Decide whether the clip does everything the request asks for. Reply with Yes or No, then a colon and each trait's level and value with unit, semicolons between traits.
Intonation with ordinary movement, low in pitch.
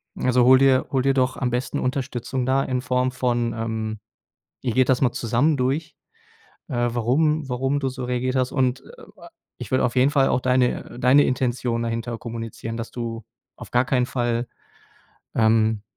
No: narrow, 1.8 semitones; low, 125 Hz